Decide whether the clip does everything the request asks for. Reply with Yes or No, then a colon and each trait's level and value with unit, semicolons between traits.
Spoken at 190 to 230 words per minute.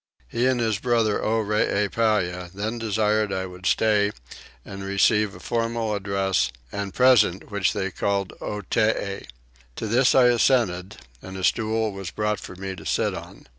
No: average, 155 wpm